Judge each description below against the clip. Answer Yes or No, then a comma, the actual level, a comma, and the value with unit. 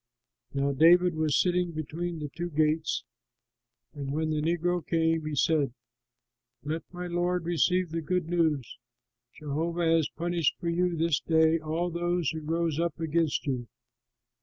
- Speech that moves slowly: No, average, 150 wpm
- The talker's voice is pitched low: No, medium, 165 Hz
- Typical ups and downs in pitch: No, narrow, 2.1 semitones